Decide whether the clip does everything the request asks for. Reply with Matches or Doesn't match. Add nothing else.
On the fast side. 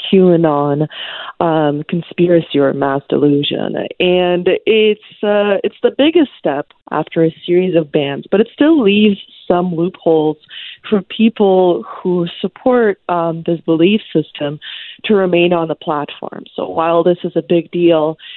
Doesn't match